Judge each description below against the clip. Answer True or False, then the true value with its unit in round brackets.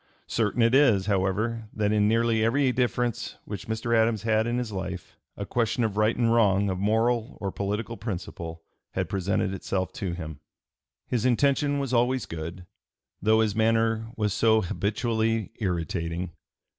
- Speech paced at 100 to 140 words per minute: False (155 wpm)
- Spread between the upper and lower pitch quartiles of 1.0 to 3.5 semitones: True (3.1 semitones)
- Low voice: True (110 Hz)